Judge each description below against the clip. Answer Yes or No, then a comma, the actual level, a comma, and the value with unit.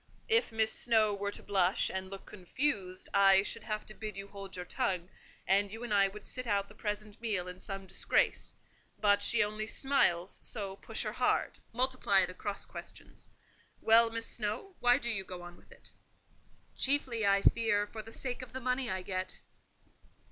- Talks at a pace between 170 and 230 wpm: Yes, average, 190 wpm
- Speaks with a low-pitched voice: No, high, 210 Hz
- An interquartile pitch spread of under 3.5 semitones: Yes, average, 3.1 semitones